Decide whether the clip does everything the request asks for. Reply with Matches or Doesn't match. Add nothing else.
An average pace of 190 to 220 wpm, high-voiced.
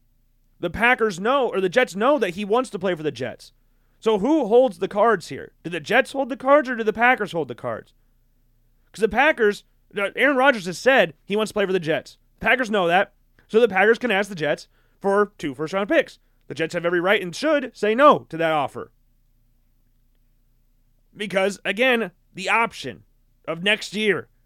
Matches